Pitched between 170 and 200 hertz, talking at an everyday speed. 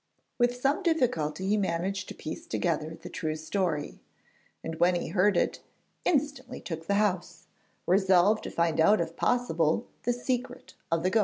Yes: high, 190 Hz; average, 165 wpm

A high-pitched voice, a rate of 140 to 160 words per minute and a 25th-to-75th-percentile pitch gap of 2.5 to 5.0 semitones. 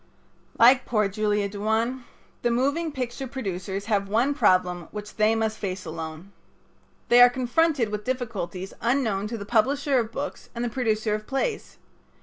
Yes: high, 225 Hz; average, 155 wpm; average, 3.9 semitones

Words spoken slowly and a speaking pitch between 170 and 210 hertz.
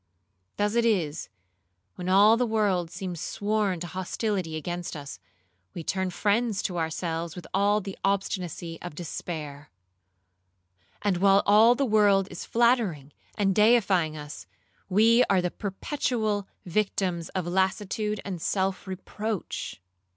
Yes: slow, 130 wpm; high, 190 Hz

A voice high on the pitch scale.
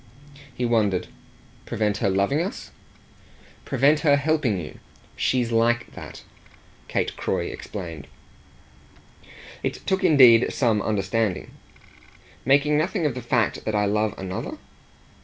No: low, 115 Hz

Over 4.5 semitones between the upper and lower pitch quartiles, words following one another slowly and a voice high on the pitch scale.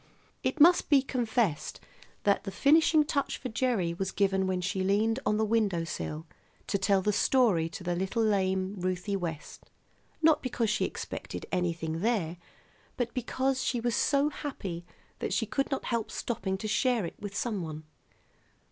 No: average, 4.9 semitones; average, 165 wpm; high, 205 Hz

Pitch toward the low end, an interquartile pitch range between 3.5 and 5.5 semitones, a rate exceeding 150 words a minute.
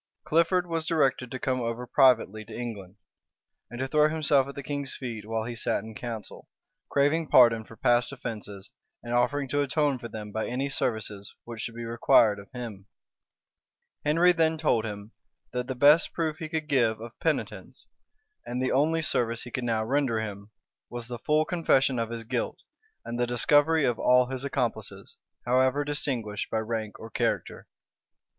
Yes: low, 125 Hz; average, 4.1 semitones; average, 180 wpm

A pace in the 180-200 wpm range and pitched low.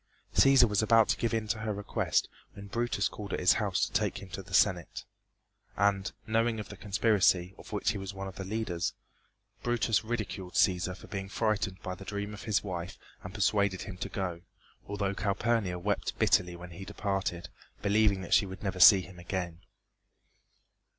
Yes: average, 190 wpm; low, 100 Hz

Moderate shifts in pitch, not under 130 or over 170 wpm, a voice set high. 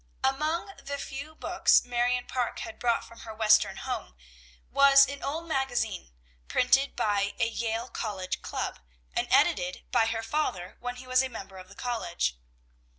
Yes: average, 4.0 semitones; average, 160 wpm; high, 245 Hz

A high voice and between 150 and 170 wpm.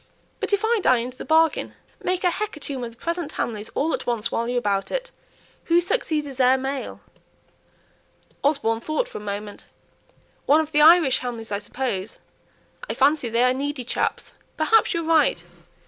No: very high, 275 Hz; average, 180 wpm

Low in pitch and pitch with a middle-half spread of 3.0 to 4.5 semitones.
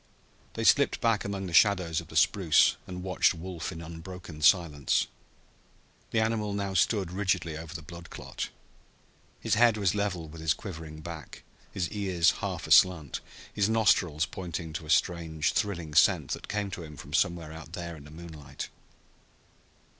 Yes: very low, 85 Hz; average, 3.4 semitones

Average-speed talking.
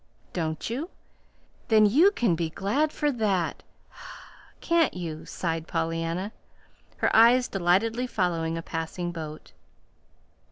No: slow, 115 wpm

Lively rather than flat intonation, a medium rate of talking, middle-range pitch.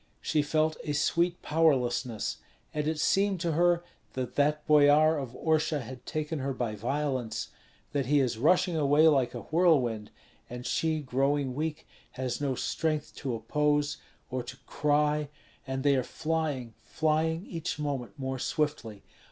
No: average, 3.2 semitones; average, 150 wpm; medium, 145 Hz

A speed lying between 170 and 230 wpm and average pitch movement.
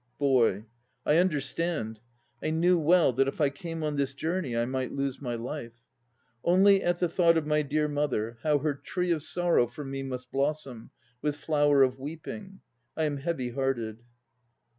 Yes: average, 175 wpm; average, 3.8 semitones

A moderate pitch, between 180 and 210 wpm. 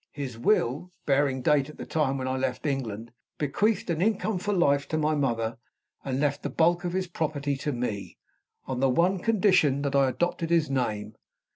Yes: medium, 145 Hz; average, 190 wpm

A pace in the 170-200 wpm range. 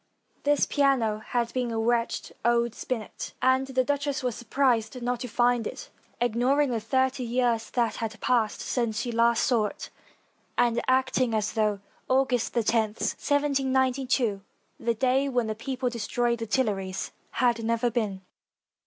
No: average, 155 wpm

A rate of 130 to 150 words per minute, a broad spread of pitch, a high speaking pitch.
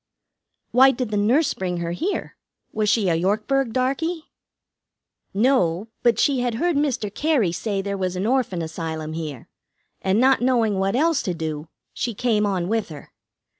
No: average, 170 wpm; wide, 6.3 semitones; high, 210 Hz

